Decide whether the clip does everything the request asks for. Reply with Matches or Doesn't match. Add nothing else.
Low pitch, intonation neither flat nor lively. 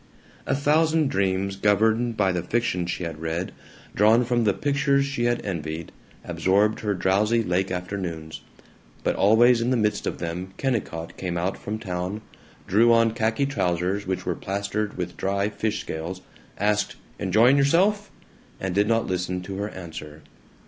Matches